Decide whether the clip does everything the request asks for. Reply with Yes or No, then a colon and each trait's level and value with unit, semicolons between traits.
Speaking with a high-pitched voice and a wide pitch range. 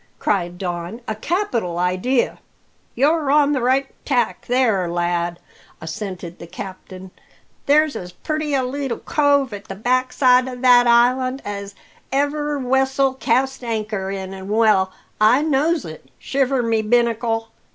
Yes: high, 240 Hz; wide, 5.7 semitones